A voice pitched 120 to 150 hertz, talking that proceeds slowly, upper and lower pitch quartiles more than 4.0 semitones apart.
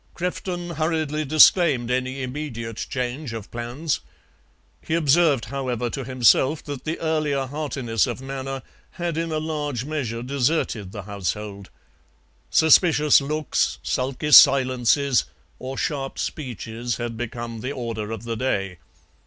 Yes: low, 135 Hz; slow, 130 wpm; average, 4.4 semitones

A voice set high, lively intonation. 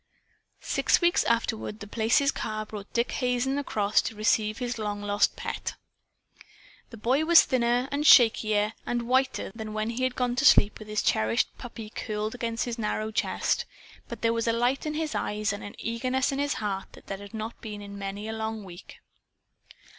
No: high, 225 Hz; average, 2.8 semitones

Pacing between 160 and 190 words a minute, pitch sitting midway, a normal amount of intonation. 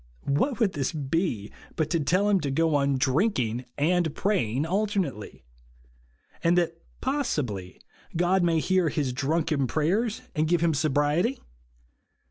No: slow, 135 wpm; medium, 160 Hz; average, 5.0 semitones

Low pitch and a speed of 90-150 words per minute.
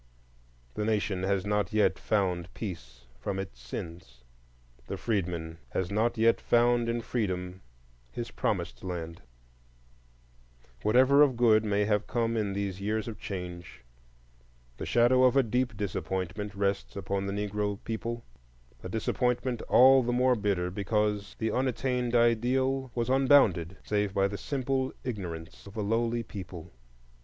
Yes: low, 105 Hz; average, 140 wpm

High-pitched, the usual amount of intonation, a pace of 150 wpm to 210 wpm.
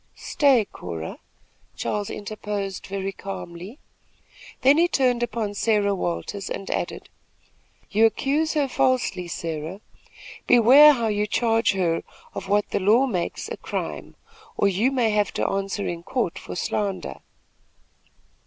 No: high, 210 Hz; average, 3.9 semitones; slow, 135 wpm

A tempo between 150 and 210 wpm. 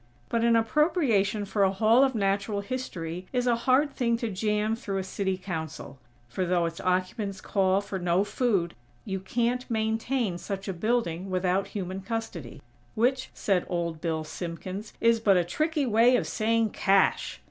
Yes: average, 170 wpm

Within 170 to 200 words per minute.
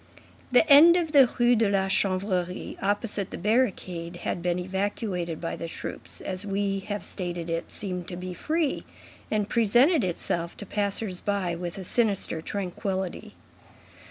No: average, 155 wpm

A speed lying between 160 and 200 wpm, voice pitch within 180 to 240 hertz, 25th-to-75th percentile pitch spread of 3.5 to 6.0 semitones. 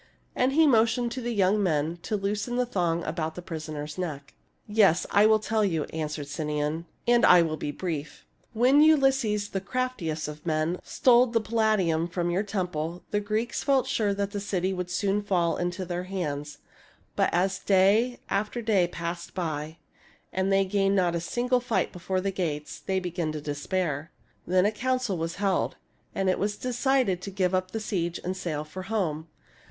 Yes: average, 185 wpm; medium, 185 Hz; average, 4.4 semitones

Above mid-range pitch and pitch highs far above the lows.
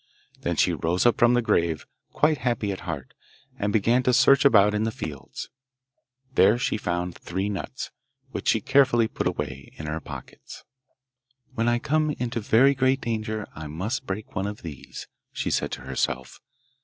No: low, 110 Hz; wide, 5.7 semitones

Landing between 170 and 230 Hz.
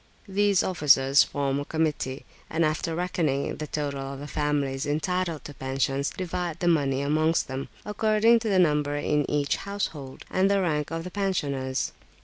No: medium, 150 Hz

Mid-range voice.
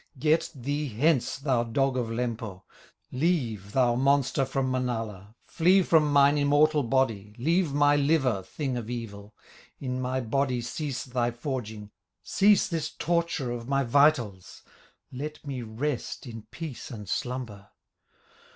No: low, 130 Hz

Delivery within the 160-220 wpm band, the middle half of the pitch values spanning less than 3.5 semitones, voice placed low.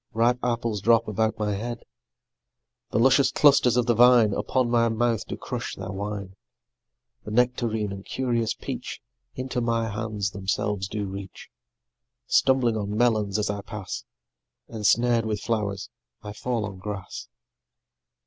No: average, 140 wpm; narrow, 2.6 semitones; low, 110 Hz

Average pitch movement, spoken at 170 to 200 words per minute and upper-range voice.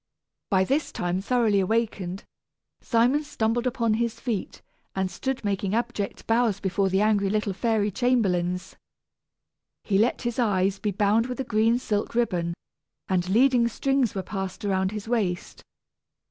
No: average, 3.7 semitones; average, 145 wpm; high, 215 Hz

